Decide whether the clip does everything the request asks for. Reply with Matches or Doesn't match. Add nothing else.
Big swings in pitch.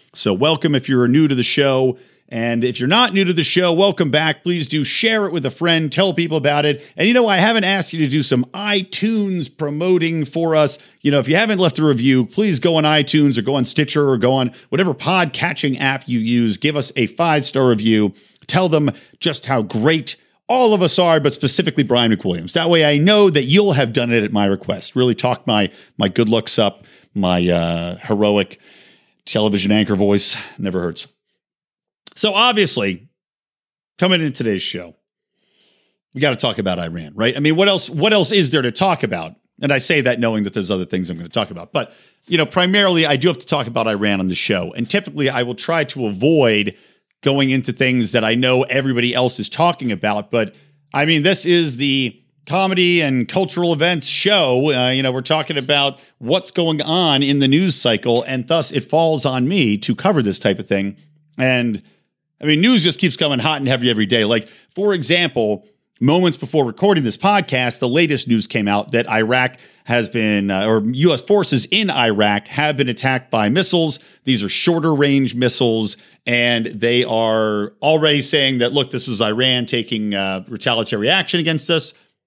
Matches